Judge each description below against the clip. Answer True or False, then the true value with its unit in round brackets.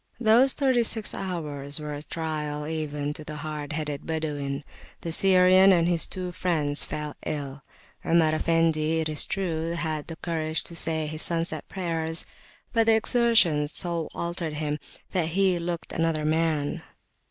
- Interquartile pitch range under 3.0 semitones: True (2.5 semitones)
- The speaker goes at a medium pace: True (160 wpm)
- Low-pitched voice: False (160 Hz)